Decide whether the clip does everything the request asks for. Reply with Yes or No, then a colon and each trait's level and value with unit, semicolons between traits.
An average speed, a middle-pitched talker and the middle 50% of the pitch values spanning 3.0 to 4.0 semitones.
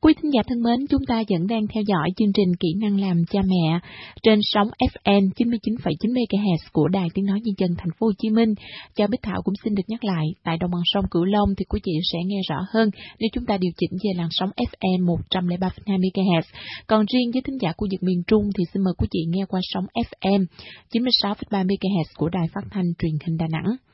No: average, 235 wpm; high, 195 Hz; average, 3.6 semitones